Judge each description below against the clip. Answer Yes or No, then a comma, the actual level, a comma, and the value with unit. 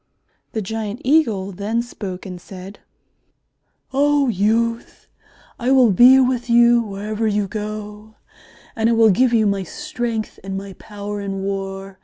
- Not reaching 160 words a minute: Yes, average, 145 wpm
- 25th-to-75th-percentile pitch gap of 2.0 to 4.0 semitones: Yes, average, 3.1 semitones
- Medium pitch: No, high, 215 Hz